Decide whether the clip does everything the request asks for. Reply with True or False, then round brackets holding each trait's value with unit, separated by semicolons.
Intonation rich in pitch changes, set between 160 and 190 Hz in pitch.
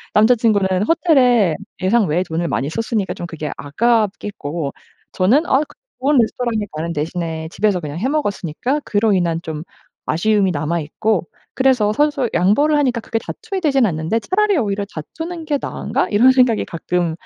False (7.2 semitones; 210 Hz)